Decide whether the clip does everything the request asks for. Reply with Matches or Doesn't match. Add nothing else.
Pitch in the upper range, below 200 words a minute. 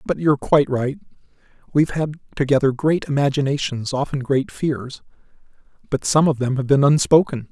Doesn't match